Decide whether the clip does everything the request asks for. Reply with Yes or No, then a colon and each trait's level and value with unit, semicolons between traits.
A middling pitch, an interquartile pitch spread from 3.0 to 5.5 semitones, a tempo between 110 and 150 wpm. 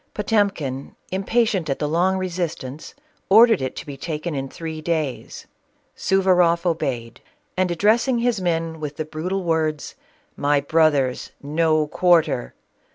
Yes: medium, 165 Hz; average, 3.9 semitones; slow, 135 wpm